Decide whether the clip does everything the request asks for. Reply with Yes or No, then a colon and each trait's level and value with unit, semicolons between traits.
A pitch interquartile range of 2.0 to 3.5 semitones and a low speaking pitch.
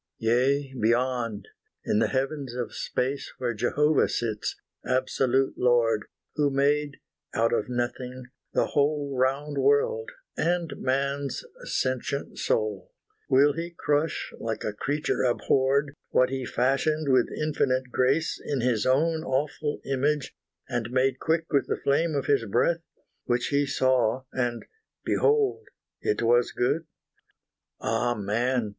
Yes: average, 3.1 semitones; low, 130 Hz